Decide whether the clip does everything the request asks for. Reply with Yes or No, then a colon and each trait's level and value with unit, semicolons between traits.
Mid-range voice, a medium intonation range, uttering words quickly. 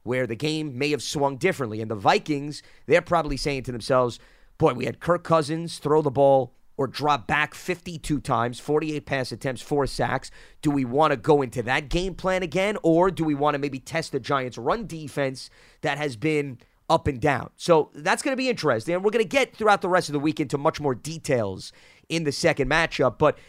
Yes: medium, 150 Hz; average, 3.5 semitones; fast, 220 wpm